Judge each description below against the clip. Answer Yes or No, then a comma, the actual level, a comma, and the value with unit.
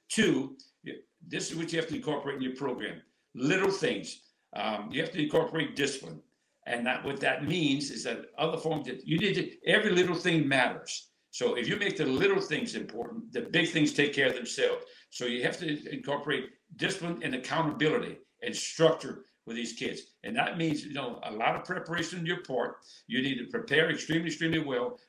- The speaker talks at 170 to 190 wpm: No, average, 200 wpm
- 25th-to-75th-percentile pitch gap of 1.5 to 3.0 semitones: No, average, 3.6 semitones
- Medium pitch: Yes, medium, 160 Hz